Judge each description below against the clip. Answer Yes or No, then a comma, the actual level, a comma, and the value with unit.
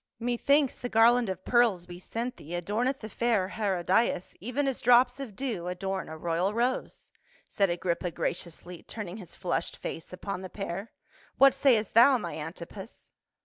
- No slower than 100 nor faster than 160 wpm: No, average, 170 wpm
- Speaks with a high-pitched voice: Yes, high, 205 Hz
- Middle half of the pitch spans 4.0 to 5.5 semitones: Yes, average, 5.2 semitones